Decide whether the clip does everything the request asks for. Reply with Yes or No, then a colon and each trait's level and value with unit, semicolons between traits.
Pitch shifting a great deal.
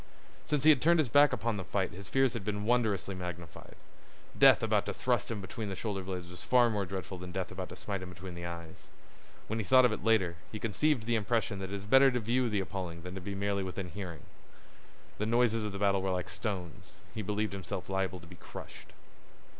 No: average, 3.5 semitones